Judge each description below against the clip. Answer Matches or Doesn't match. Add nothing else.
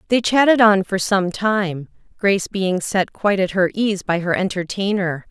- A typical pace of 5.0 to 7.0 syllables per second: Doesn't match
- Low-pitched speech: Doesn't match